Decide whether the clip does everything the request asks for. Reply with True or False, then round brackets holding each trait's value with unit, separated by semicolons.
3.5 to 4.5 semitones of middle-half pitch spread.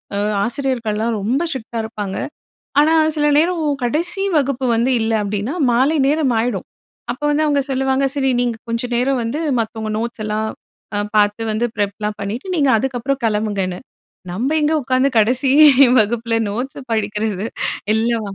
True (4.0 semitones)